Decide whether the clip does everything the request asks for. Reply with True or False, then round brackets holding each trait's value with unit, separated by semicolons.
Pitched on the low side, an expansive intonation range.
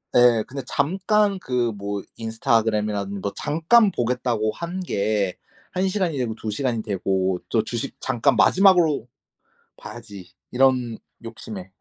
True (115 Hz; 5.7 semitones)